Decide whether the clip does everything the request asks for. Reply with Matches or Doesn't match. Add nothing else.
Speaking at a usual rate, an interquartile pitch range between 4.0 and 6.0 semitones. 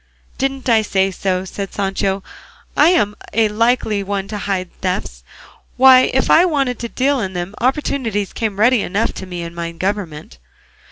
Matches